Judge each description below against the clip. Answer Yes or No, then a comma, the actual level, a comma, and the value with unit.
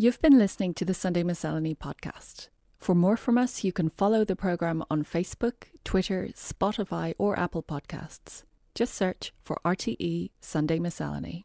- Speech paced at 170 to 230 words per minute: No, average, 155 wpm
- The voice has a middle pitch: Yes, medium, 180 Hz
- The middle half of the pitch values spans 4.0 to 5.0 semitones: No, average, 3.6 semitones